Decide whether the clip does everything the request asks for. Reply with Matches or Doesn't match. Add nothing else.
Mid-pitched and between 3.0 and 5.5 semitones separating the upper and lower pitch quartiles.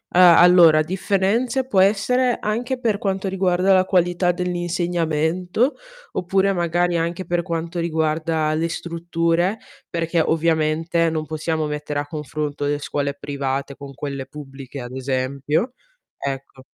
Matches